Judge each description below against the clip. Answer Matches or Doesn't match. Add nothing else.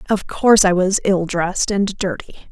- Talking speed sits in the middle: Matches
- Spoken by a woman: Matches